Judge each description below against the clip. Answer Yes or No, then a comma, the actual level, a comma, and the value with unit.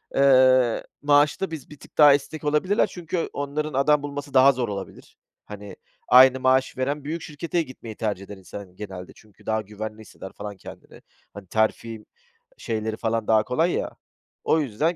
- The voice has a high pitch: No, low, 130 Hz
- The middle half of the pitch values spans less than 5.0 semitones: No, average, 5.3 semitones